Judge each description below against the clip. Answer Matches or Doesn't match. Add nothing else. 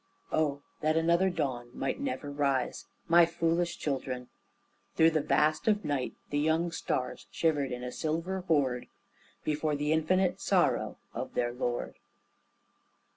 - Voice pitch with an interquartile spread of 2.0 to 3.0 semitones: Doesn't match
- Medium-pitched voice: Matches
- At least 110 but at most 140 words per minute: Matches